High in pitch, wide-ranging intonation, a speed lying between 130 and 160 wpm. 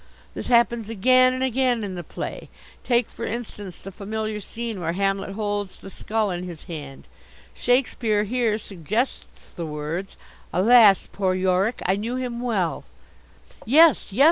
No: high, 210 Hz; average, 4.1 semitones; average, 155 wpm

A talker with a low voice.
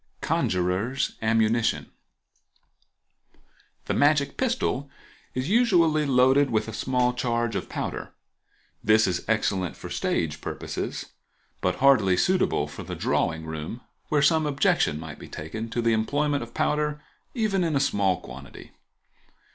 Yes: low, 120 Hz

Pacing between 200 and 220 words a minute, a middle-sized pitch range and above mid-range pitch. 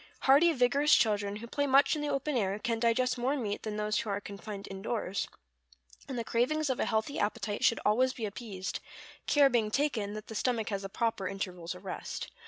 Yes: fast, 205 wpm; average, 4.1 semitones; high, 225 Hz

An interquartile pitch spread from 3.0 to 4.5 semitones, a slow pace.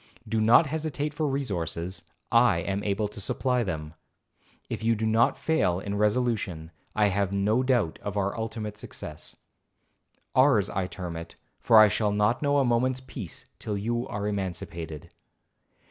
No: average, 4.1 semitones; average, 155 wpm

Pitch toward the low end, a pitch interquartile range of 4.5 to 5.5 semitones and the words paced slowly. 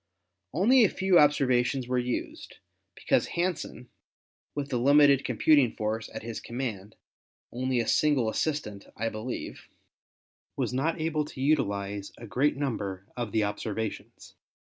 No: low, 125 Hz; average, 5.1 semitones; average, 145 wpm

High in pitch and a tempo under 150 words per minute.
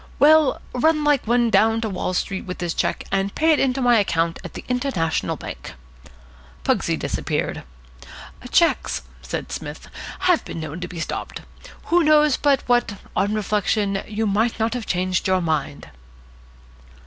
No: high, 220 Hz; average, 160 wpm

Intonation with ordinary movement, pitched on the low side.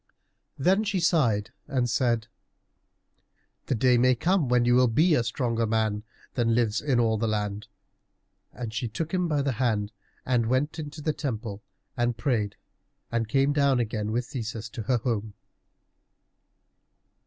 Yes: average, 3.7 semitones; low, 120 Hz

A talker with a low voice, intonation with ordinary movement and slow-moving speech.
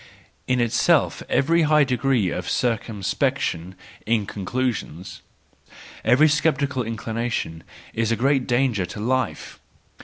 Yes: low, 120 Hz; average, 4.2 semitones; slow, 110 wpm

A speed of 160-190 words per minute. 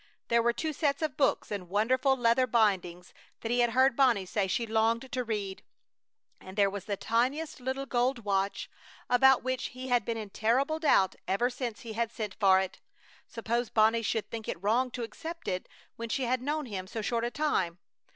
No: average, 200 wpm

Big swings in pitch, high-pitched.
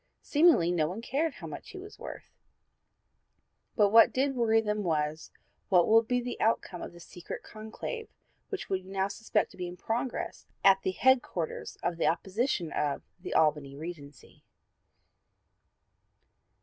Yes: wide, 5.8 semitones; high, 195 Hz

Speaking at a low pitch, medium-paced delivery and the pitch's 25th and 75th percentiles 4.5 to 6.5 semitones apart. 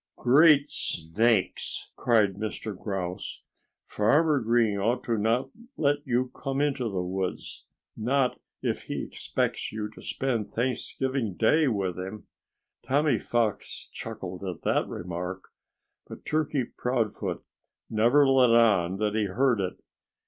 No: low, 115 Hz; slow, 125 wpm; average, 5.1 semitones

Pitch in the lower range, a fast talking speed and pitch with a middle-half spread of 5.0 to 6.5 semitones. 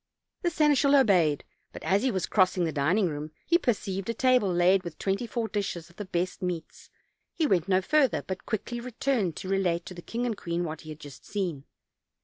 No: high, 190 Hz; fast, 215 wpm; average, 5.3 semitones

